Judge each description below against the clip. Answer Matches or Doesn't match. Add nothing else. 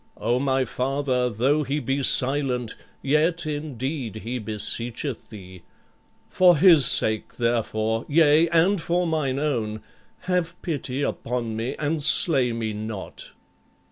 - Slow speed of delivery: Matches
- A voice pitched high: Doesn't match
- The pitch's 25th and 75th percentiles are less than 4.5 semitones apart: Doesn't match